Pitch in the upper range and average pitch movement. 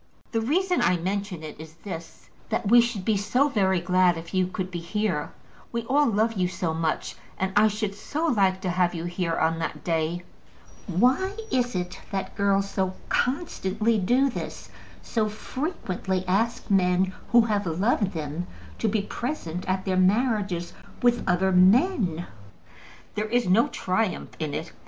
Yes: high, 195 Hz; average, 4.1 semitones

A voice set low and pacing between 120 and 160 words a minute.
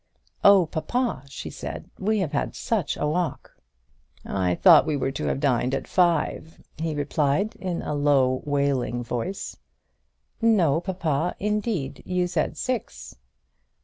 No: medium, 155 Hz; average, 145 wpm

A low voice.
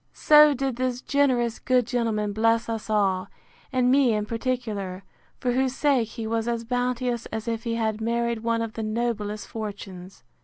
No: high, 230 Hz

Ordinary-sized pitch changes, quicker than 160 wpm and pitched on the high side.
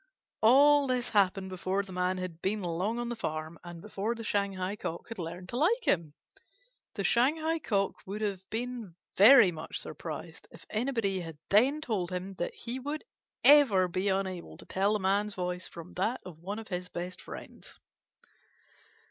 Yes: average, 4.5 semitones; average, 175 wpm; high, 195 Hz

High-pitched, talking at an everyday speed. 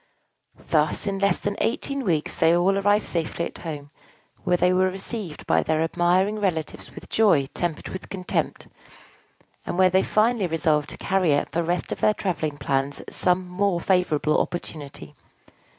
No: medium, 180 Hz; average, 165 wpm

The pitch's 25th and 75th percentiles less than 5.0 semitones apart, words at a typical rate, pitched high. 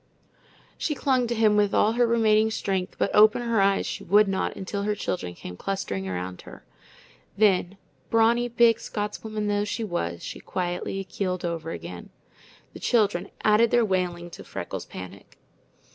Yes: average, 3.6 semitones; average, 160 wpm; high, 205 Hz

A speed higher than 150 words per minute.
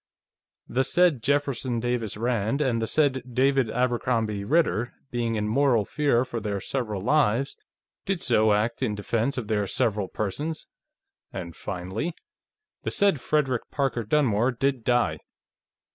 No: average, 145 wpm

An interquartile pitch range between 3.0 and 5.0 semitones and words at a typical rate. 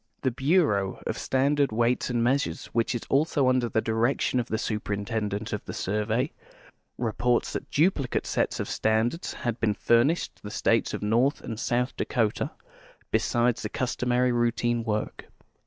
No: narrow, 2.6 semitones; average, 150 wpm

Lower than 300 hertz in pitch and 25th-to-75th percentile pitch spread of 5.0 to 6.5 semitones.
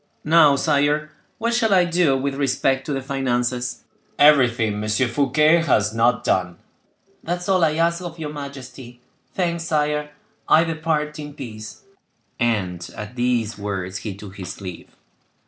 Yes: low, 135 Hz; average, 5.3 semitones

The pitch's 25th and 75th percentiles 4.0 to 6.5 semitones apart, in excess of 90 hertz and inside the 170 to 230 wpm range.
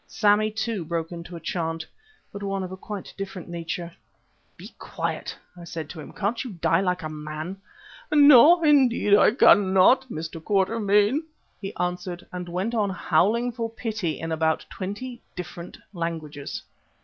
No: average, 4.3 semitones; high, 190 Hz; average, 155 wpm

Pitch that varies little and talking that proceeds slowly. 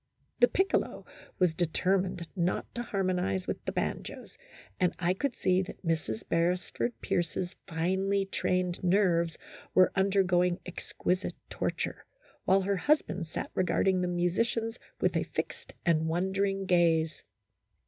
Yes: narrow, 2.1 semitones; slow, 130 wpm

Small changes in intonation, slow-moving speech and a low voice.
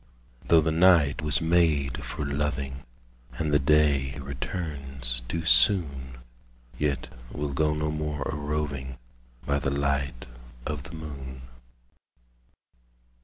Yes: narrow, 2.0 semitones; slow, 120 wpm; very low, 70 Hz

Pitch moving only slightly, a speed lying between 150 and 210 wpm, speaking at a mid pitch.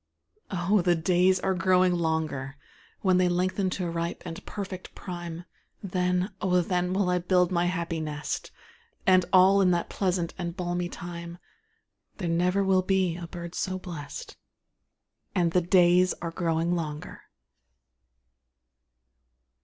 No: narrow, 1.5 semitones; average, 140 wpm; medium, 180 Hz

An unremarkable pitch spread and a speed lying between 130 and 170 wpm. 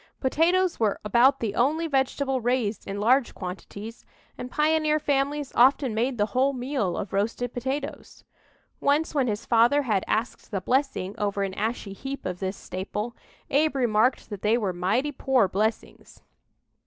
Yes: average, 4.9 semitones; average, 155 wpm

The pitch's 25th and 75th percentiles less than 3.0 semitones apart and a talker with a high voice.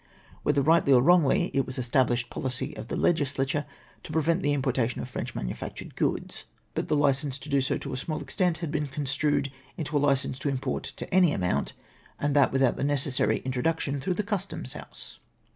No: narrow, 2.6 semitones; medium, 140 Hz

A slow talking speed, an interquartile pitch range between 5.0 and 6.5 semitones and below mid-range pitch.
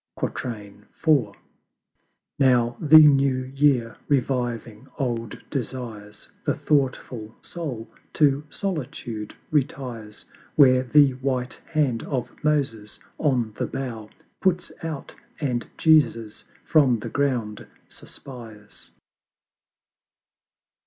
No: slow, 90 wpm; average, 3.7 semitones; low, 130 Hz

